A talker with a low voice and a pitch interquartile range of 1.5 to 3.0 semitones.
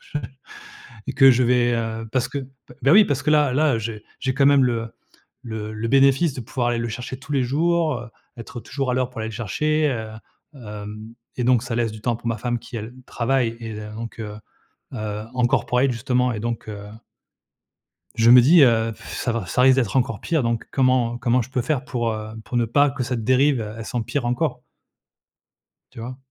Yes: low, 120 Hz; average, 2.7 semitones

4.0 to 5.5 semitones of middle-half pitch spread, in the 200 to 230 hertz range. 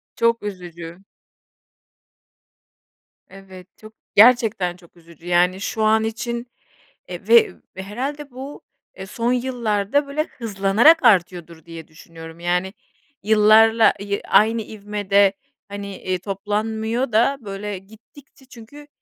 No: average, 3.6 semitones; high, 210 Hz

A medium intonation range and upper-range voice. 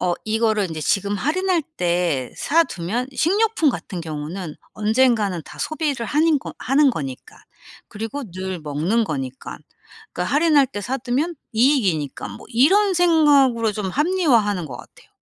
No: wide, 8.6 semitones; high, 225 Hz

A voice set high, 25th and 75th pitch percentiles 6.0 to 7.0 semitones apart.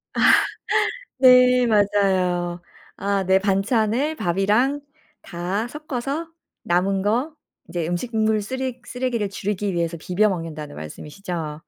No: high, 200 Hz; wide, 5.6 semitones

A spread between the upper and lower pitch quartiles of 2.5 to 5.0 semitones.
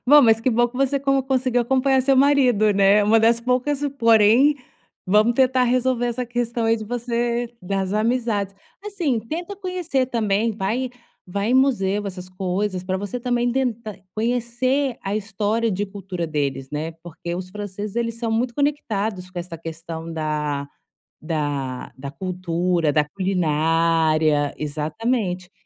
No: wide, 5.4 semitones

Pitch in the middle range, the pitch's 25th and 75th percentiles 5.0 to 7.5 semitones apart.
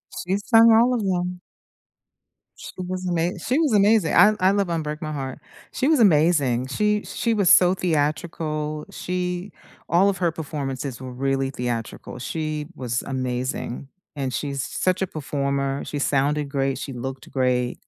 Yes: medium, 155 Hz; average, 5.3 semitones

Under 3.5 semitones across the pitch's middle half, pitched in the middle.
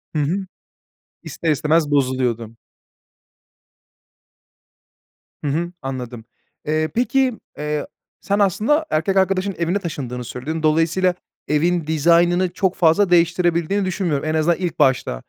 No: average, 3.9 semitones; medium, 165 Hz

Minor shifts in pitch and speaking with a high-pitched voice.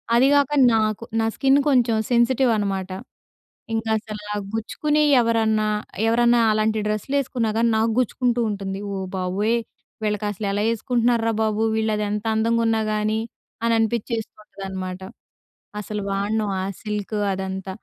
Yes: narrow, 2.0 semitones; high, 220 Hz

